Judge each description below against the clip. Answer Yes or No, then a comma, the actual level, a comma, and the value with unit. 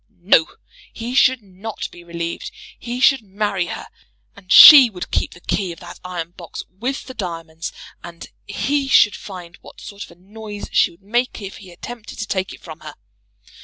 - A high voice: Yes, high, 195 Hz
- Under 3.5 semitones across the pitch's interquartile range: No, average, 4.6 semitones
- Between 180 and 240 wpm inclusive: Yes, average, 190 wpm